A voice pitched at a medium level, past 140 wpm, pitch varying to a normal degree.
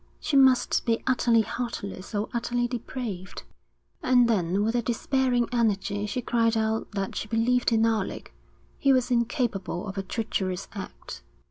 No: high, 230 Hz; average, 150 wpm; average, 3.2 semitones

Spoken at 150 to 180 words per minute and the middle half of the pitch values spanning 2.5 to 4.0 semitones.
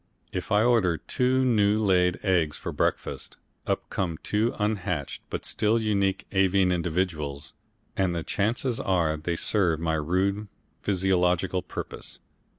No: slow, 135 wpm; average, 3.4 semitones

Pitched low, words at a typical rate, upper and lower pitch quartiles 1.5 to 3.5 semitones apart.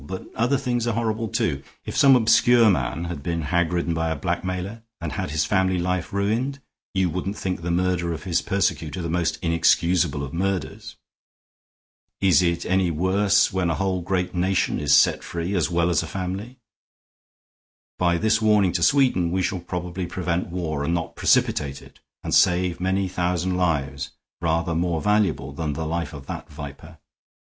Yes: very low, 90 Hz; average, 175 wpm; narrow, 2.5 semitones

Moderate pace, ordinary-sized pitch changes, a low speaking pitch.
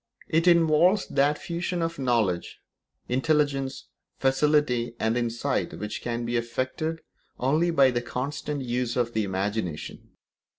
No: slow, 125 wpm; average, 4.3 semitones; low, 130 Hz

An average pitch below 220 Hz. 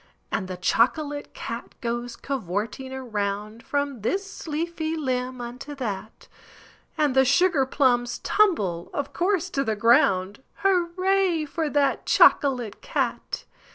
No: very high, 265 Hz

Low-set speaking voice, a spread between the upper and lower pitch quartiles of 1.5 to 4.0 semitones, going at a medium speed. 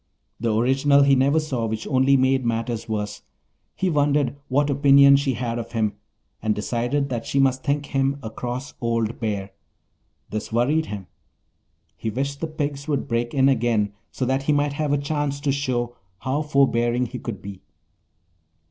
Yes: low, 130 Hz; average, 3.3 semitones; average, 175 wpm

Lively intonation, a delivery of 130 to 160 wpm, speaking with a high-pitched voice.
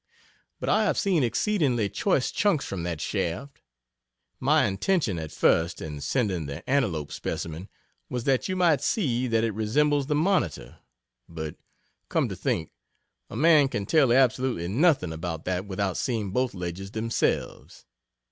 No: wide, 8.3 semitones; average, 150 wpm; low, 115 Hz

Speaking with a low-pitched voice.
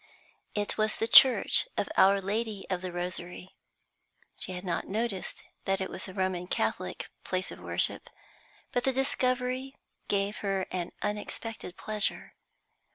No: high, 200 Hz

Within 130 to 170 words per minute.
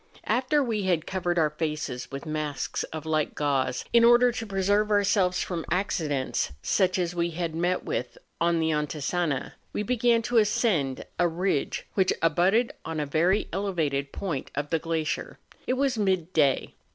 Yes: average, 165 wpm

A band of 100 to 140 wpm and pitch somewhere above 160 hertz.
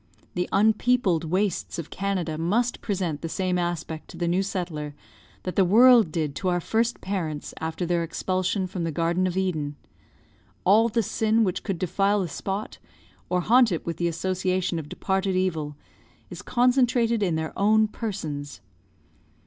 No: average, 165 wpm; medium, 185 Hz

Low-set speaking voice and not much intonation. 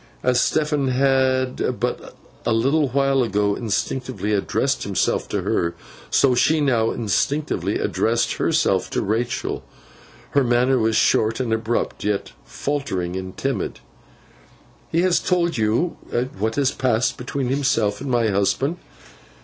No: low, 125 Hz; average, 3.8 semitones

